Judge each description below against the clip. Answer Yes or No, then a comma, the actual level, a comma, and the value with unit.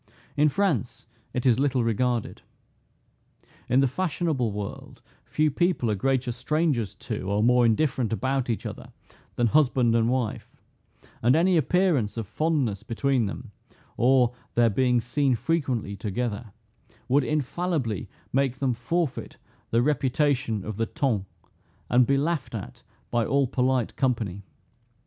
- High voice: No, low, 125 Hz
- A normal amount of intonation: Yes, average, 3.6 semitones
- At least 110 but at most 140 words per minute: Yes, slow, 135 wpm